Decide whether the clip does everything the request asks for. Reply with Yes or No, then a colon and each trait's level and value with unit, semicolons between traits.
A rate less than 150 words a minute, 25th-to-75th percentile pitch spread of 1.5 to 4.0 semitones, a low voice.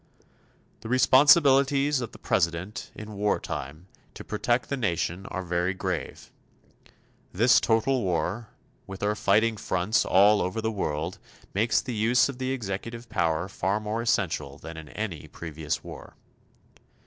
No: average, 140 wpm; average, 4.8 semitones; low, 105 Hz